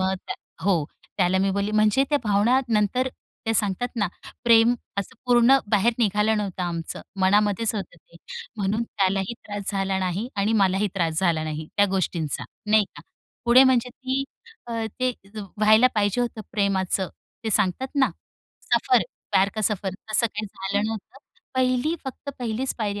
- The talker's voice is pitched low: No, high, 210 Hz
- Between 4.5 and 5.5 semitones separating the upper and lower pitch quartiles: No, average, 3.4 semitones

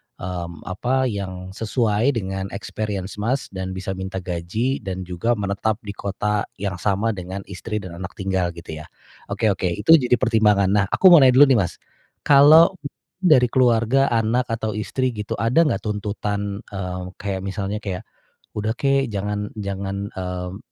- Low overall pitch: Yes, low, 105 Hz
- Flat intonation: No, average, 3.3 semitones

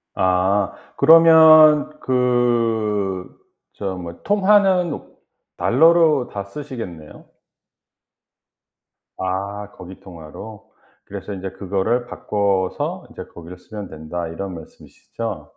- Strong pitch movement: Yes, wide, 6.1 semitones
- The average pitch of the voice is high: No, low, 105 Hz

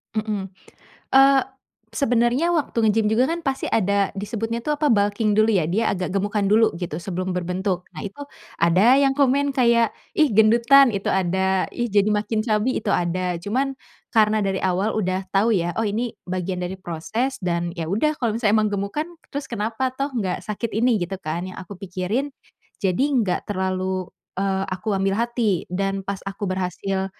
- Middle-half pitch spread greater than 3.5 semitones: Yes, average, 3.9 semitones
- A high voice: Yes, high, 205 Hz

